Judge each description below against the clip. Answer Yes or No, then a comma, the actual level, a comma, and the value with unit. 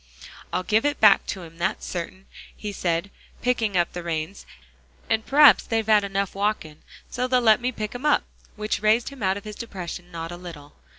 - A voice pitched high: Yes, high, 200 Hz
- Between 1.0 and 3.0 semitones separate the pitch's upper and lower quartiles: No, average, 4.1 semitones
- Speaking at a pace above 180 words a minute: Yes, average, 200 wpm